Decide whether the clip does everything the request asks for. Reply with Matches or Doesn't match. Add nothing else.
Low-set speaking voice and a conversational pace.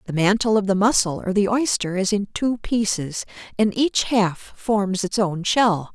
Doesn't match